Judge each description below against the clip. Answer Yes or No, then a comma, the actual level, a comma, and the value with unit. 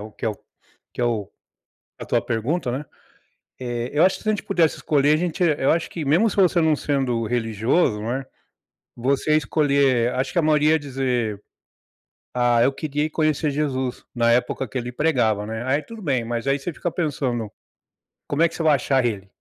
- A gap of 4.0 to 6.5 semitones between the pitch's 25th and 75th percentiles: Yes, average, 4.4 semitones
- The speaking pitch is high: No, low, 135 Hz